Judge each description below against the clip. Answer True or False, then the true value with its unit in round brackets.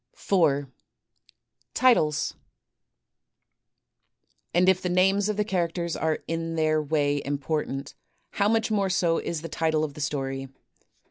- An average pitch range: True (3.9 semitones)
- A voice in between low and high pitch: True (165 Hz)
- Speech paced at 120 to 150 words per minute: True (135 wpm)